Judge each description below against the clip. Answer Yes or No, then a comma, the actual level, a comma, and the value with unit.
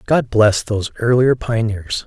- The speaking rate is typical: Yes, average, 145 wpm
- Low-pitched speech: Yes, low, 115 Hz